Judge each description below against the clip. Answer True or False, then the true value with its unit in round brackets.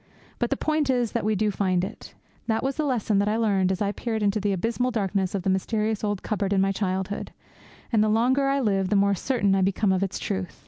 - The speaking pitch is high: True (205 Hz)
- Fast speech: True (245 wpm)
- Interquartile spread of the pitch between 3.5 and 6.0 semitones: False (2.8 semitones)